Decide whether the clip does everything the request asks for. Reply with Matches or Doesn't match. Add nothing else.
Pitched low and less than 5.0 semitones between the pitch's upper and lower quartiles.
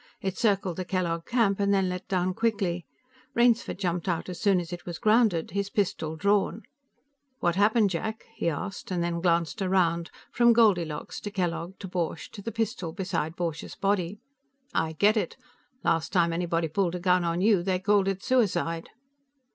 Doesn't match